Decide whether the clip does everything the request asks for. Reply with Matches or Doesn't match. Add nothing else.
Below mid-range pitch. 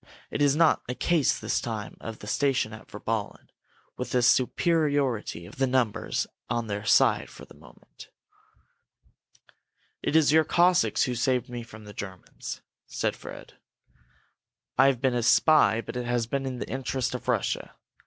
Matches